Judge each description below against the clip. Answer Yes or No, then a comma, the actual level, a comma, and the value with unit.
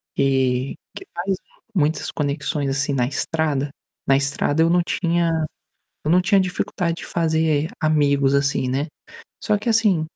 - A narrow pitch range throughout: No, average, 3.5 semitones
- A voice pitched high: No, medium, 155 Hz